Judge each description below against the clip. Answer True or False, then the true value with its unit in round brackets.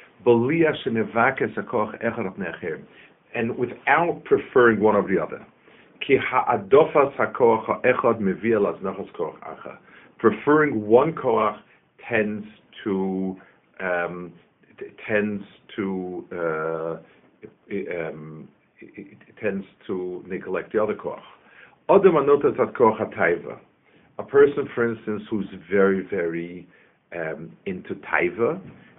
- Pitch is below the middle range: True (100 Hz)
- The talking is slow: True (70 wpm)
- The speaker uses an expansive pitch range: False (4.8 semitones)